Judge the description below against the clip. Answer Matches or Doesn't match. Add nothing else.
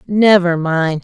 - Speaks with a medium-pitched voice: Matches